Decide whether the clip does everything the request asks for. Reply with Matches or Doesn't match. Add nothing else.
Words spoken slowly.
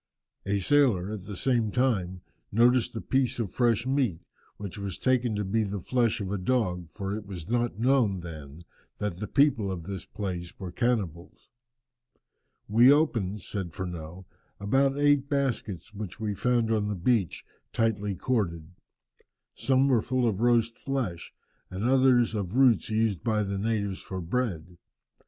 Doesn't match